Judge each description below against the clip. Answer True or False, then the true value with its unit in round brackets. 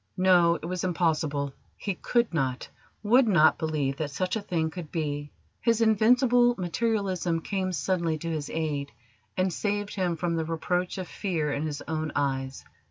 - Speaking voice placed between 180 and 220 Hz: False (170 Hz)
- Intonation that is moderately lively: True (3.8 semitones)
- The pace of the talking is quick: False (165 wpm)